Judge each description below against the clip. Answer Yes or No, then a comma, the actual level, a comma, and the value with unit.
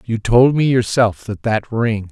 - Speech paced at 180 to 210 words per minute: Yes, average, 200 wpm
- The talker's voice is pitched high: No, low, 115 Hz